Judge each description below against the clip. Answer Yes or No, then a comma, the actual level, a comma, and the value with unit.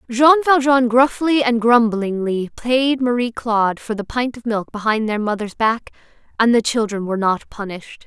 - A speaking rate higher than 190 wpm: No, average, 170 wpm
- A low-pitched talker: No, high, 230 Hz